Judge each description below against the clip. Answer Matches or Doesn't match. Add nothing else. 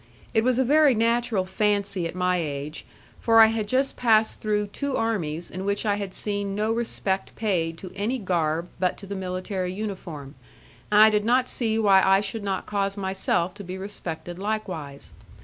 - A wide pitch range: Doesn't match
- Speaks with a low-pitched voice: Doesn't match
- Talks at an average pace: Matches